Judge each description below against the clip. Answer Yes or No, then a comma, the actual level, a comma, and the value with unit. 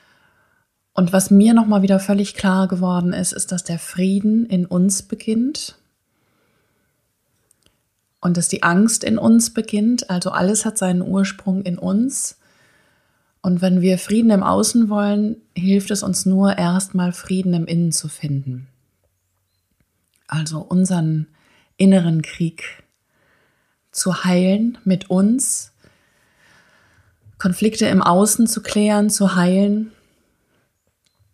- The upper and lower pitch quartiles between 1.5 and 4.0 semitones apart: Yes, average, 3.1 semitones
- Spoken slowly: Yes, slow, 120 wpm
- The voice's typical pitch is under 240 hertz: Yes, high, 190 Hz